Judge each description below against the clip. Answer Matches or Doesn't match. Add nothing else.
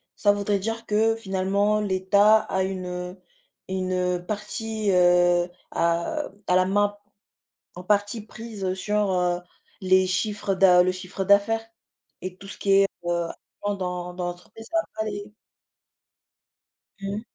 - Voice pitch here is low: Doesn't match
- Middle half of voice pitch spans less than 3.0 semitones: Matches